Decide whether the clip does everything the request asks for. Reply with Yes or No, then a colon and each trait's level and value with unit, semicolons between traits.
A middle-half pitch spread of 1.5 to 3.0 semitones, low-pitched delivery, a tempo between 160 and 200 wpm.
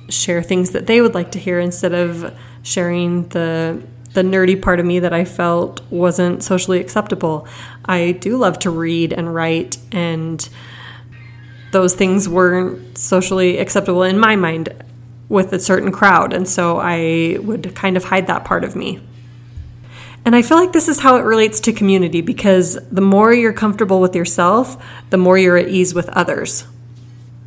No: average, 2.7 semitones; medium, 180 Hz; average, 175 wpm